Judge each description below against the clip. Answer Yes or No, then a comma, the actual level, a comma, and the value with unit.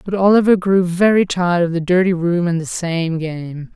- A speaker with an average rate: No, fast, 210 wpm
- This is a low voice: No, medium, 175 Hz